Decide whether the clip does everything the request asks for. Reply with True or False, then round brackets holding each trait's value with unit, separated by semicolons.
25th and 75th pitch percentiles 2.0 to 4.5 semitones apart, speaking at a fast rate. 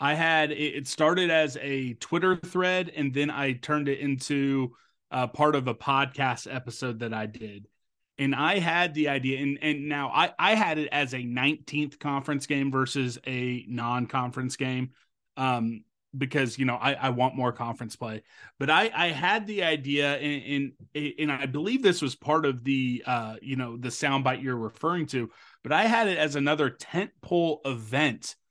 False (2.9 semitones; 180 wpm)